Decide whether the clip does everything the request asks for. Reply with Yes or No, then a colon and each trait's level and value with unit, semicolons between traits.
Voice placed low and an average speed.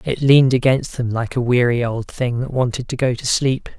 No: low, 125 Hz; fast, 240 wpm